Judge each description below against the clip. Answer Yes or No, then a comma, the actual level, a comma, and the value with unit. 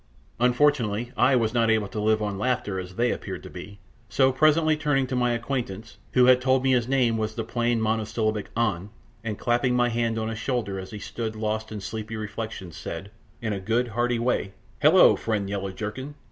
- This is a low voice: Yes, low, 115 Hz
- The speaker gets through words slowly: No, average, 200 wpm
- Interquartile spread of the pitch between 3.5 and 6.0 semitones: No, average, 2.7 semitones